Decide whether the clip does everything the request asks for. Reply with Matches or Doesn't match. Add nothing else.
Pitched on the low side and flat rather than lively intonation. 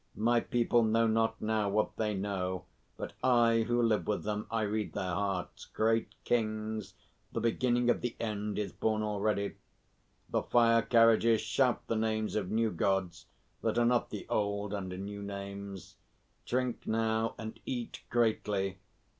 Matches